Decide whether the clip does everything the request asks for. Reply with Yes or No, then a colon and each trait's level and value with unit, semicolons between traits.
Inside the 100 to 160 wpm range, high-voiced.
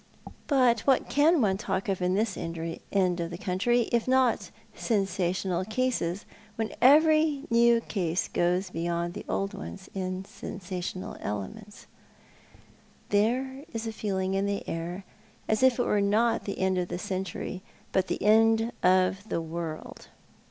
Yes: average, 150 wpm; high, 195 Hz